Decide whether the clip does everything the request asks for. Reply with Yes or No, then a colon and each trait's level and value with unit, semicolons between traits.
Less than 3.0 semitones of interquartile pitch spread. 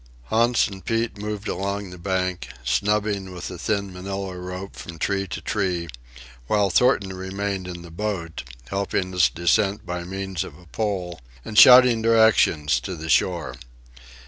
Yes: narrow, 2.6 semitones